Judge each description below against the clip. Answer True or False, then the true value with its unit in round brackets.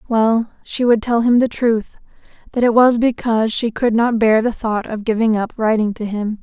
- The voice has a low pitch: False (225 Hz)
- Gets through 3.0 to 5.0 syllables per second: True (4.8 syllables/s)